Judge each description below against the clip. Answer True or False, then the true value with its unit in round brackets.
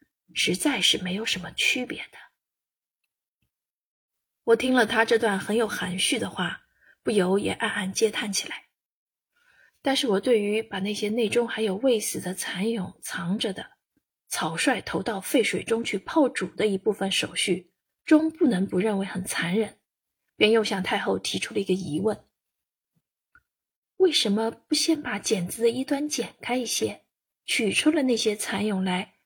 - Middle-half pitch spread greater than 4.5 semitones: False (4.0 semitones)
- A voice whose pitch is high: True (220 Hz)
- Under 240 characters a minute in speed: True (230 characters per minute)